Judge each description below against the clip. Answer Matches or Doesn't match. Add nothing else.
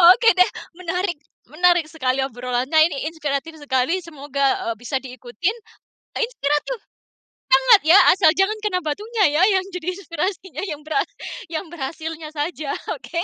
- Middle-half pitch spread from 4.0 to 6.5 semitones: Matches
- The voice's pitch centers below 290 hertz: Doesn't match